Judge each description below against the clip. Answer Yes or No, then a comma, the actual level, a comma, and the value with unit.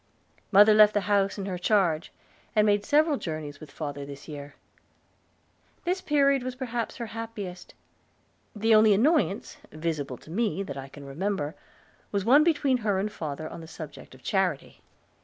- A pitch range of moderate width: No, wide, 6.5 semitones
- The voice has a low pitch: No, high, 200 Hz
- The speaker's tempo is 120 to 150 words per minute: No, average, 165 wpm